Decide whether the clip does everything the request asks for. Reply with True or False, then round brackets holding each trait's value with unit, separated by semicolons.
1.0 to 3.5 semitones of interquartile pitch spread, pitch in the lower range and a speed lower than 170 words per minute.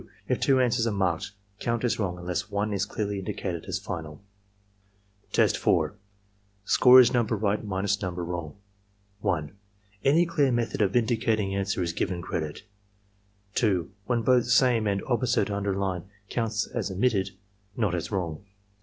False (4.2 semitones; 100 Hz; 155 wpm)